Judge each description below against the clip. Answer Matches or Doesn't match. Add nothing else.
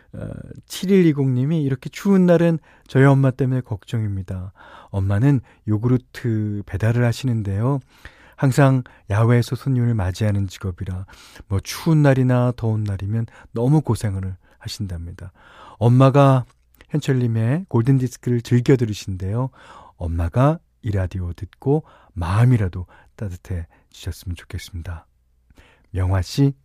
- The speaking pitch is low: Matches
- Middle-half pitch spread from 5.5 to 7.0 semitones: Matches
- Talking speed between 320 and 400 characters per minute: Doesn't match